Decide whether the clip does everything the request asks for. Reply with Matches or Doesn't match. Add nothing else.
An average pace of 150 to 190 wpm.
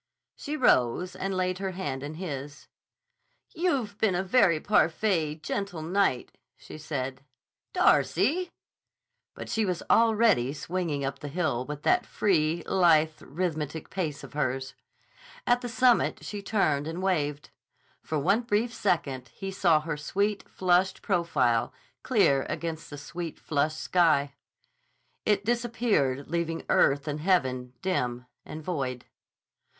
Doesn't match